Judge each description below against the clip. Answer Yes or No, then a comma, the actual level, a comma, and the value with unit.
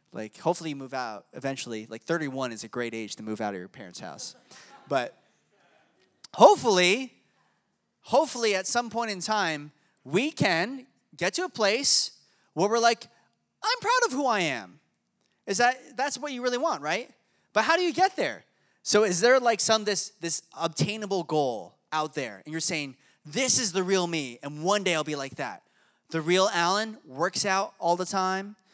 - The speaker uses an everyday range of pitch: No, wide, 7.5 semitones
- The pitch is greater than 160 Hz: Yes, high, 190 Hz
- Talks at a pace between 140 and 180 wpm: No, average, 190 wpm